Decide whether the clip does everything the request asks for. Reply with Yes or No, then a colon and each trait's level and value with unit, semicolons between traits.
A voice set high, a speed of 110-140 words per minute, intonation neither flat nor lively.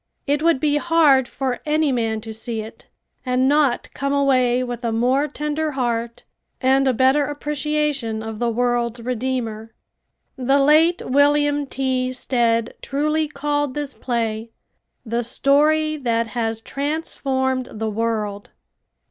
Yes: very high, 260 Hz; slow, 135 wpm; average, 3.8 semitones